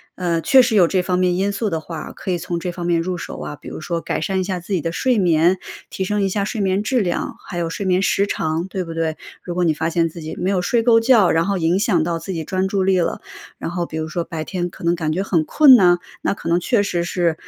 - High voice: No, medium, 180 Hz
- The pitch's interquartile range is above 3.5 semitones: No, average, 2.8 semitones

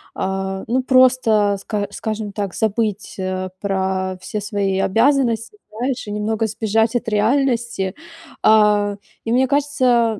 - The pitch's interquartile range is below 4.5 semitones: Yes, average, 2.9 semitones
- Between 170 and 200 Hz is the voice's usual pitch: No, high, 215 Hz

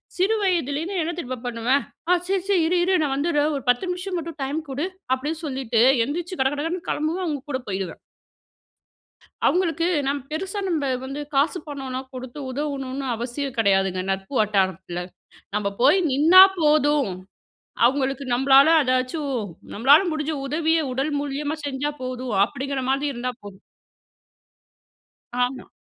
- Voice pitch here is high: Yes, very high, 280 Hz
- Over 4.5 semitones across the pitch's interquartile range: No, average, 3.8 semitones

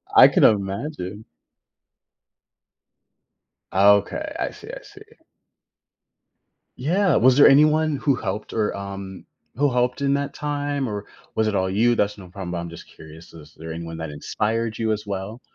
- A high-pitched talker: No, low, 105 Hz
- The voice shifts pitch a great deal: Yes, wide, 6.1 semitones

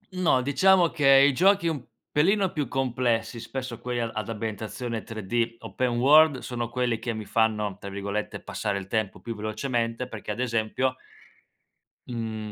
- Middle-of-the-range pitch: No, low, 120 Hz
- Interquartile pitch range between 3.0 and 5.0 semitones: Yes, average, 3.4 semitones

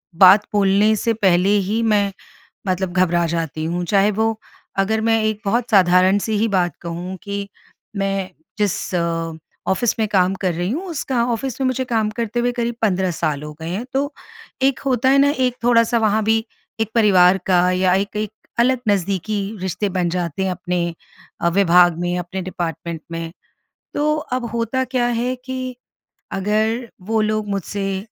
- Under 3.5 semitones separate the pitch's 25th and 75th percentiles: No, average, 4.0 semitones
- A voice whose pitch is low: No, high, 200 Hz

